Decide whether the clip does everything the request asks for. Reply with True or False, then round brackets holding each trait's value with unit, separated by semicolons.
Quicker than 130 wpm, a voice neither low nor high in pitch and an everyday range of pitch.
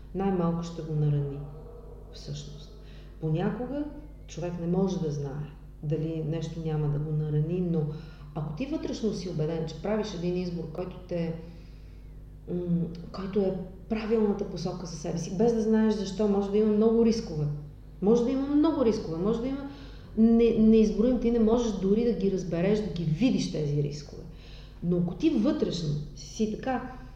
False (160 wpm; 180 Hz; 5.7 semitones)